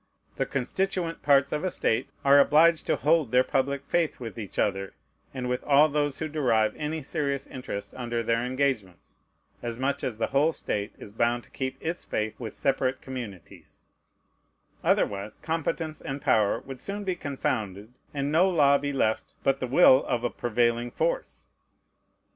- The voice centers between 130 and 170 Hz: Yes, low, 135 Hz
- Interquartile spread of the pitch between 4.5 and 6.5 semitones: No, average, 4.1 semitones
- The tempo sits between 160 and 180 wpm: Yes, average, 170 wpm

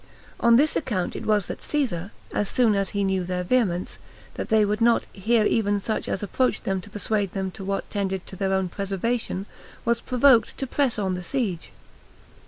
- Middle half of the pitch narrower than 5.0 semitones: Yes, average, 3.5 semitones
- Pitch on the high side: Yes, high, 205 Hz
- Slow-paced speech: No, average, 195 wpm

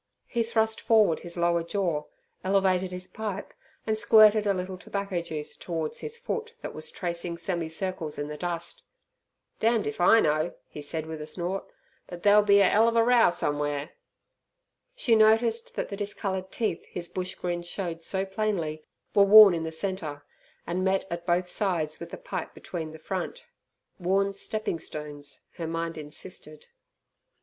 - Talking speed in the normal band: Yes, average, 170 wpm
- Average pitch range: Yes, average, 4.0 semitones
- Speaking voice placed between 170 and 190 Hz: Yes, medium, 185 Hz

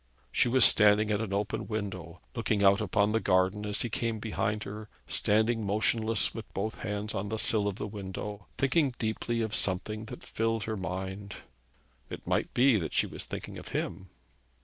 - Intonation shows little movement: Yes, narrow, 1.9 semitones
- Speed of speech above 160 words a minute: Yes, average, 185 wpm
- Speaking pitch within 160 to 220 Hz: No, low, 105 Hz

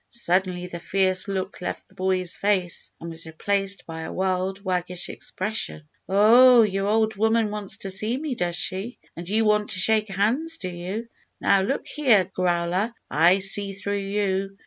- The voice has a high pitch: Yes, high, 195 Hz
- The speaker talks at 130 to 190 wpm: Yes, average, 170 wpm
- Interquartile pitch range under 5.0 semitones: Yes, narrow, 2.6 semitones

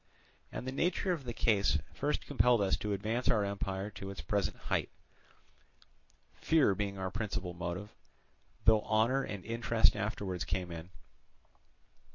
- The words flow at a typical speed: Yes, average, 145 wpm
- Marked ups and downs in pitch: No, average, 3.3 semitones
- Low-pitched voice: Yes, low, 105 Hz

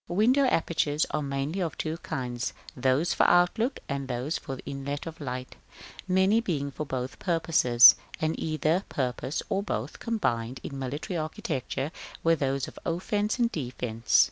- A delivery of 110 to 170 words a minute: Yes, average, 150 wpm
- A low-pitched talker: No, medium, 150 Hz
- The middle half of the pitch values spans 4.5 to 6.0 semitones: Yes, average, 5.1 semitones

